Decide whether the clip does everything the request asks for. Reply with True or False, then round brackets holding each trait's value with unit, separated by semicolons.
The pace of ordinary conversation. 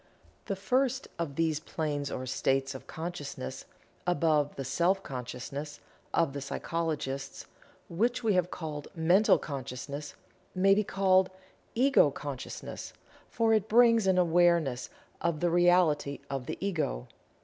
False (130 wpm)